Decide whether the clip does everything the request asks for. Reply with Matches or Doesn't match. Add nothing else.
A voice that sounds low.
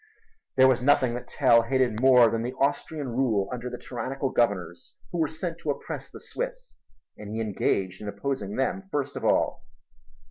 Matches